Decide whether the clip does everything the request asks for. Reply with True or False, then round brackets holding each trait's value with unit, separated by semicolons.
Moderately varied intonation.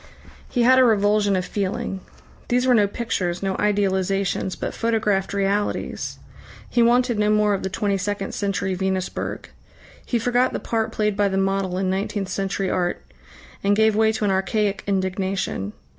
False (2.0 semitones)